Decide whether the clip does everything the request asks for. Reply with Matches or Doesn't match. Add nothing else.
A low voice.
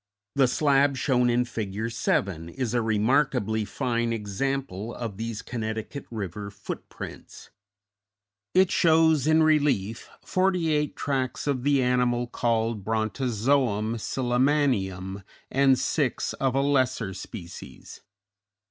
Matches